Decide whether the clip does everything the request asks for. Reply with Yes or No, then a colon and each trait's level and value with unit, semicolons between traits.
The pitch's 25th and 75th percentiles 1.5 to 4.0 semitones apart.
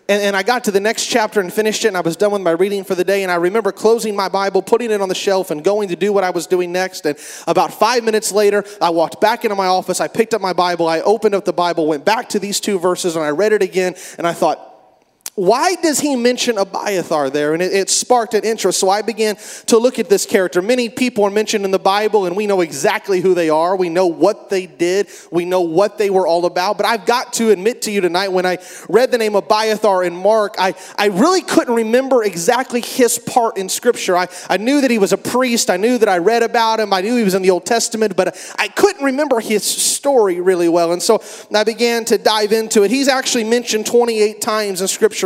Yes: average, 3.6 semitones